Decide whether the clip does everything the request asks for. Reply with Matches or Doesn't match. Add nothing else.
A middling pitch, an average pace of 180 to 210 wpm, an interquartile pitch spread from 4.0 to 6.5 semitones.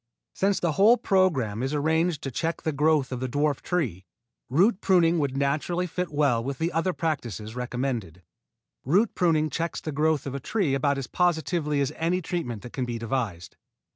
Matches